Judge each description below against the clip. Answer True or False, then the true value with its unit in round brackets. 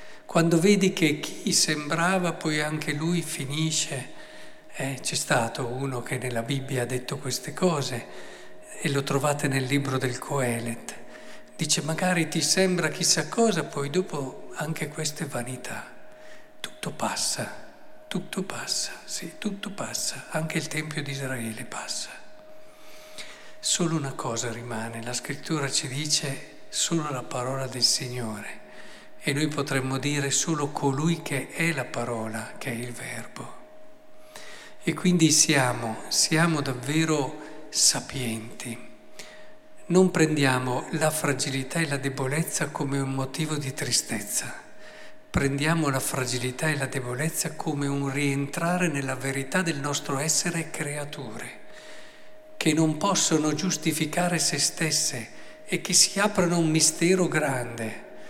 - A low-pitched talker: False (150 Hz)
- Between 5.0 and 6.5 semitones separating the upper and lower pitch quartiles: False (4.0 semitones)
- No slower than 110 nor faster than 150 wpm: True (130 wpm)